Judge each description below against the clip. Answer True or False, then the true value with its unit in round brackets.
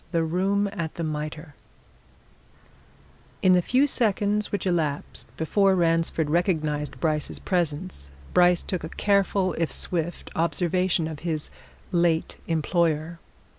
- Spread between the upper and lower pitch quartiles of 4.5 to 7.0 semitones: False (2.8 semitones)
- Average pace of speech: False (120 wpm)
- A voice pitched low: False (170 Hz)